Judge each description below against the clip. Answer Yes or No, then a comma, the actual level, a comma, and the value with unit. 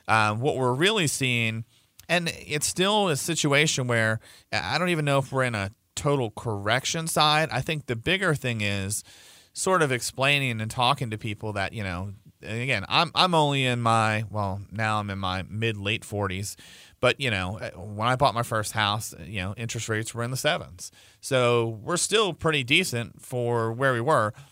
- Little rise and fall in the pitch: No, average, 5.3 semitones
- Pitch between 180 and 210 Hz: No, low, 120 Hz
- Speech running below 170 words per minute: No, average, 190 wpm